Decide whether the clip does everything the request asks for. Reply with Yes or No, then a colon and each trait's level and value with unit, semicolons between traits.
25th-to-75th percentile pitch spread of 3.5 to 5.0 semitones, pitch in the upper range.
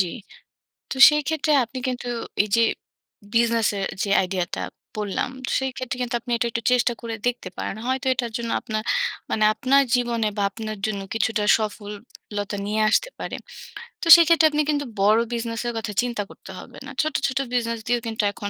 No: average, 2.9 semitones; high, 230 Hz